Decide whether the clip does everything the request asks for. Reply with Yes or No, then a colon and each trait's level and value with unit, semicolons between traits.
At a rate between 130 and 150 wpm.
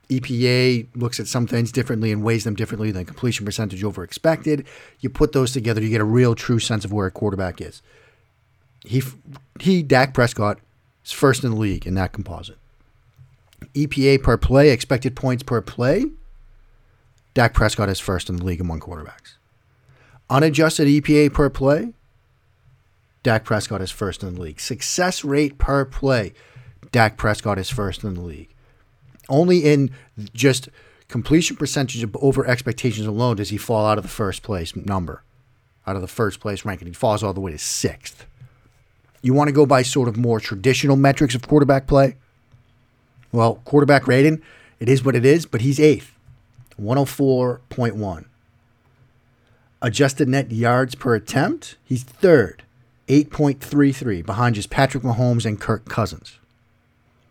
No: average, 160 wpm